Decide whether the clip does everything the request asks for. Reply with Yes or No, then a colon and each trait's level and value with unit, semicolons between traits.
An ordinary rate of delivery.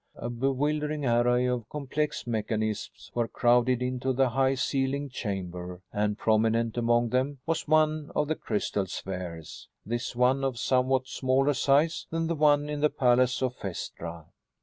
Yes: average, 150 wpm